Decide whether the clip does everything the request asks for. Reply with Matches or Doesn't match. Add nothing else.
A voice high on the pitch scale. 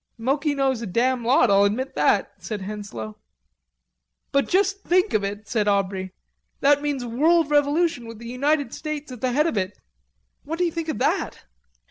Matches